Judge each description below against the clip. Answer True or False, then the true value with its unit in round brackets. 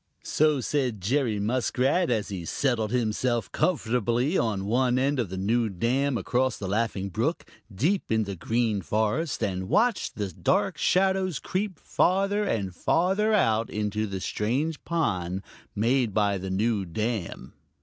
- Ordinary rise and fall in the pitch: False (5.7 semitones)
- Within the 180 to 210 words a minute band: False (150 wpm)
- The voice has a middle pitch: False (115 Hz)